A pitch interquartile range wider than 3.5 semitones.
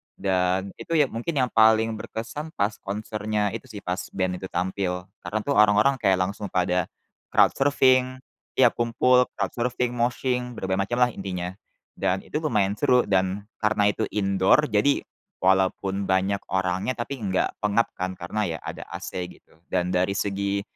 Yes: average, 4.1 semitones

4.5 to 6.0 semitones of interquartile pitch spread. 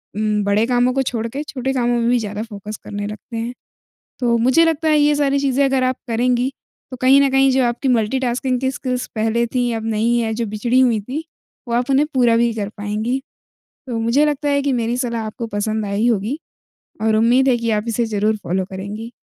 No: average, 3.1 semitones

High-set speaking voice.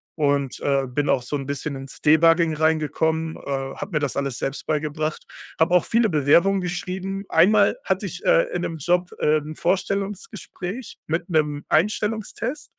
No: medium, 160 Hz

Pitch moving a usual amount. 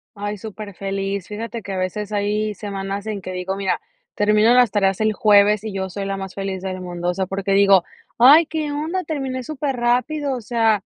Yes: average, 3.4 semitones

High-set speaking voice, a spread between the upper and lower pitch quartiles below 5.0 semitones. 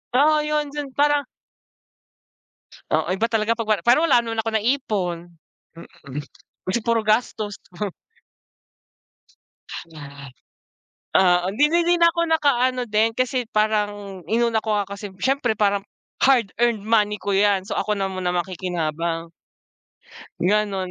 Yes: high, 215 Hz; average, 4.2 semitones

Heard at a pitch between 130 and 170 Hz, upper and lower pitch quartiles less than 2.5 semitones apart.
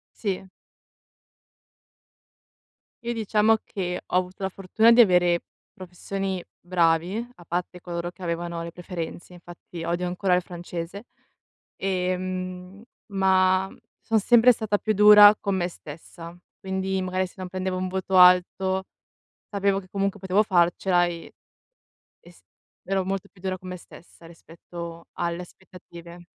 No: medium, 185 Hz; narrow, 1.8 semitones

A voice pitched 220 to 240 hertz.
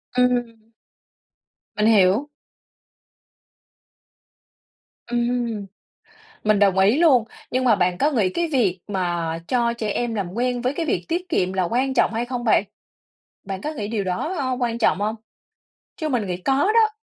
Yes: high, 230 Hz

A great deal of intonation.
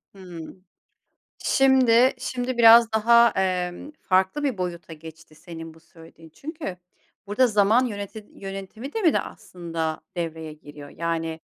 Yes: wide, 6.3 semitones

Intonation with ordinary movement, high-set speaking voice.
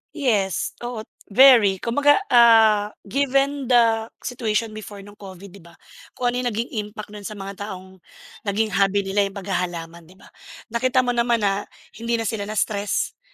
Yes: average, 3.2 semitones; high, 215 Hz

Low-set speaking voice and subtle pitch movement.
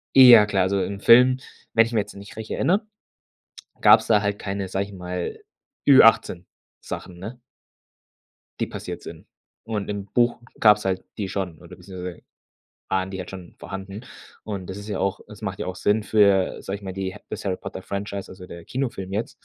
Yes: low, 100 Hz; narrow, 2.2 semitones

